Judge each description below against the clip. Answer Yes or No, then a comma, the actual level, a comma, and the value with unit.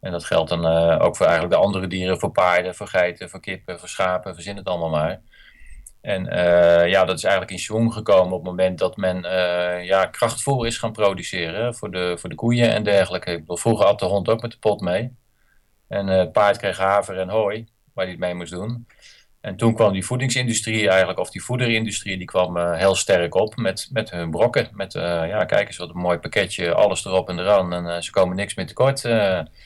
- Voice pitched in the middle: No, very low, 95 Hz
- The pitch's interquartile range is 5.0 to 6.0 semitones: No, average, 3.9 semitones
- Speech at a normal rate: No, fast, 230 wpm